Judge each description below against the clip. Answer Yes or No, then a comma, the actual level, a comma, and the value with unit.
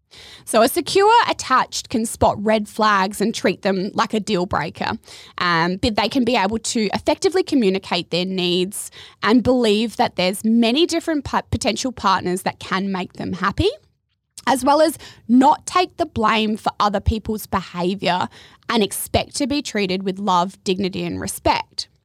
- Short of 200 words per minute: Yes, average, 165 wpm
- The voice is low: No, high, 215 Hz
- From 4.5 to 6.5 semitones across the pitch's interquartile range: Yes, average, 5.1 semitones